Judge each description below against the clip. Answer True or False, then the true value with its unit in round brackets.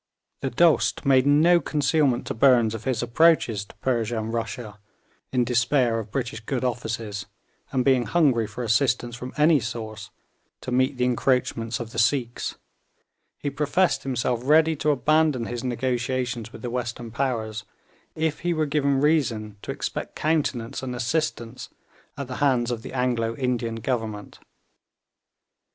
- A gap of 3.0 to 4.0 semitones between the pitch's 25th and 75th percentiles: True (3.3 semitones)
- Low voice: True (125 Hz)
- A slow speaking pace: False (150 wpm)